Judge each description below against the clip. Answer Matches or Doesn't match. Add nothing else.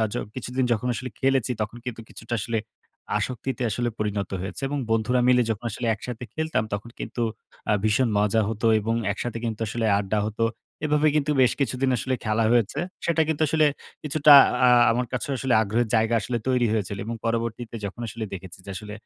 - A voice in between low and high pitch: Doesn't match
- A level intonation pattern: Doesn't match